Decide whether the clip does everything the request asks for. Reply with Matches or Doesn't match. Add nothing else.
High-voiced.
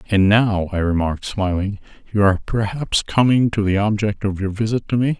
Doesn't match